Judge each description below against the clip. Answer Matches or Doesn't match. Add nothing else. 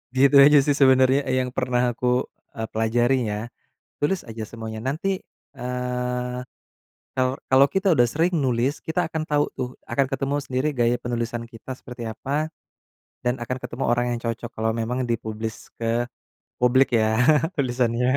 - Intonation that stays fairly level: Matches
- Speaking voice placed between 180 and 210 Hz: Doesn't match